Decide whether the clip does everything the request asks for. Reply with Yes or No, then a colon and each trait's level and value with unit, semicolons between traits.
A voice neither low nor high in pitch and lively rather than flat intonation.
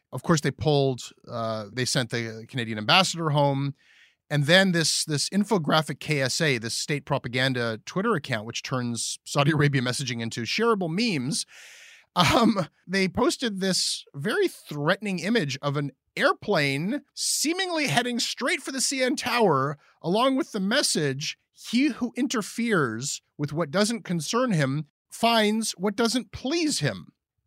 Yes: medium, 170 Hz; wide, 8.8 semitones